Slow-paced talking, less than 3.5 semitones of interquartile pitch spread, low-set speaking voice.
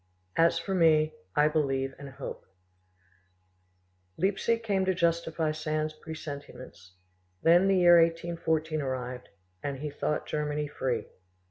No: slow, 120 wpm; average, 3.0 semitones; medium, 155 Hz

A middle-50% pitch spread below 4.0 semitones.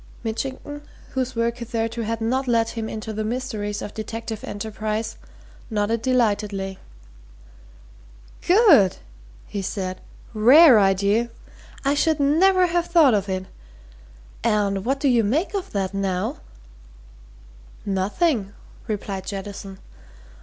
No: average, 4.3 semitones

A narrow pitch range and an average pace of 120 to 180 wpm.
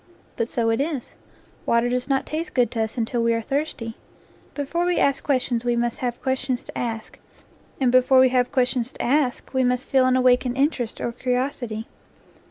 No: narrow, 2.0 semitones; average, 200 wpm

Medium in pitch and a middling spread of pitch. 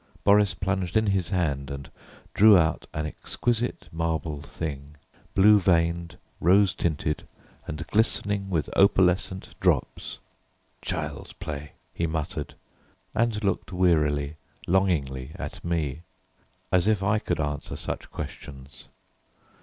No: very low, 85 Hz; average, 4.6 semitones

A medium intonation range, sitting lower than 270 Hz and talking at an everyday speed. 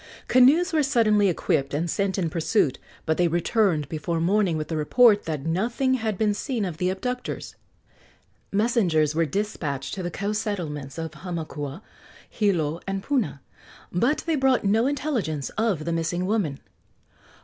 No: wide, 5.9 semitones; high, 190 Hz; average, 155 wpm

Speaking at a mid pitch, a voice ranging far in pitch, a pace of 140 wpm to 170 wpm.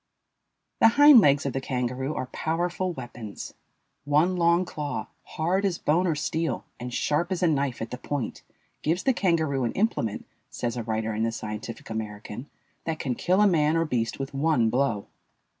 No: medium, 145 Hz; wide, 6.1 semitones; average, 180 wpm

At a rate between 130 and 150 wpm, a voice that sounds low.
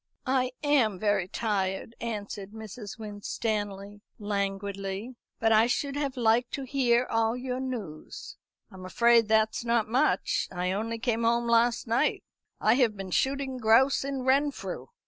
No: average, 145 wpm; high, 225 Hz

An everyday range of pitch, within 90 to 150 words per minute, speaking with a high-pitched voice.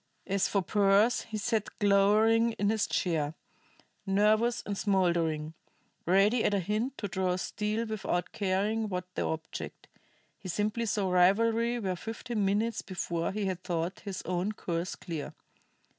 Yes: average, 3.1 semitones; average, 145 wpm; high, 200 Hz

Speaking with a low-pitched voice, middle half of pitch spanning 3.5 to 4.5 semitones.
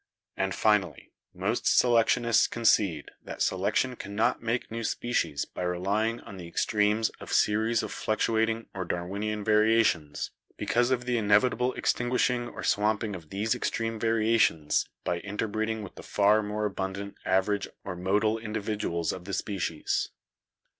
No: low, 105 Hz; average, 2.8 semitones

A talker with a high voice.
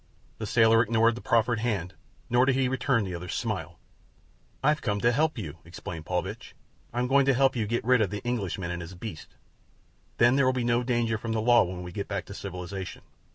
No: low, 115 Hz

